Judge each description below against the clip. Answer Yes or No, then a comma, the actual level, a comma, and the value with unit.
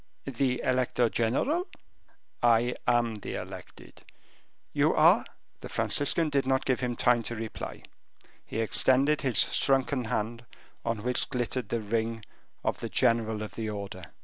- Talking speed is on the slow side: No, average, 150 wpm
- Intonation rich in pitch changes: No, narrow, 2.6 semitones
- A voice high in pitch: No, low, 120 Hz